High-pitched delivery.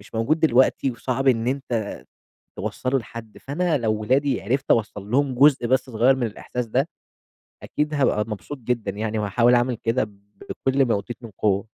No: low, 120 Hz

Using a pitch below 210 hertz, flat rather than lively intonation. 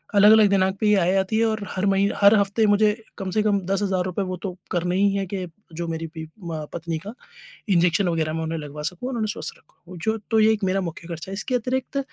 No: high, 190 Hz; average, 3.5 semitones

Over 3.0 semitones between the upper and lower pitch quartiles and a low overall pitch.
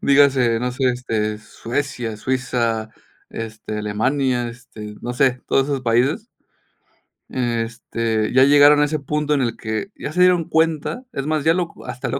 Yes: average, 4.1 semitones; low, 125 Hz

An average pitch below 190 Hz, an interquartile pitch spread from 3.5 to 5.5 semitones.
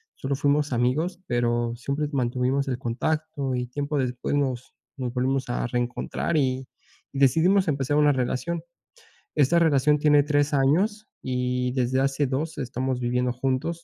No: low, 135 Hz; average, 2.9 semitones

